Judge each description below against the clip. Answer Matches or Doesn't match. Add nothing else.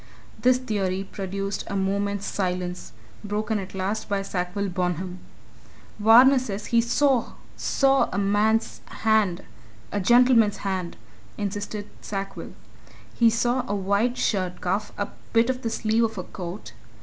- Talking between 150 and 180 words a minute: Doesn't match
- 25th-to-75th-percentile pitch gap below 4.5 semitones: Matches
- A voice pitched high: Matches